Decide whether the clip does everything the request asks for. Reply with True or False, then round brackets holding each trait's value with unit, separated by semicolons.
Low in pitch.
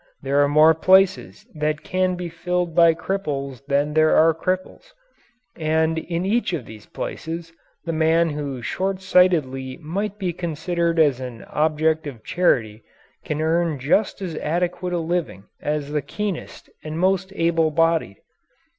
False (160 Hz)